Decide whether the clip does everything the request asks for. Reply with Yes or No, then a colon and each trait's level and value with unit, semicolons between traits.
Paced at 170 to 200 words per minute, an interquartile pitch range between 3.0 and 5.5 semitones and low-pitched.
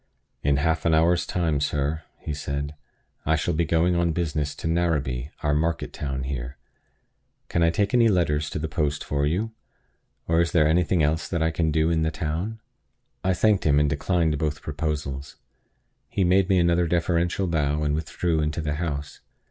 No: average, 185 wpm; narrow, 2.6 semitones; very low, 80 Hz